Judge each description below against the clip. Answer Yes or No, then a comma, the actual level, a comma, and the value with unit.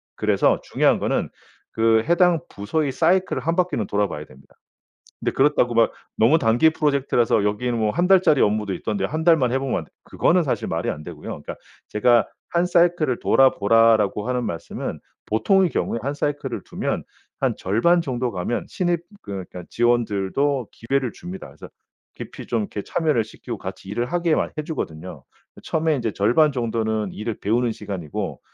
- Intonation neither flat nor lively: No, wide, 6.9 semitones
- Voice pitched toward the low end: Yes, low, 120 Hz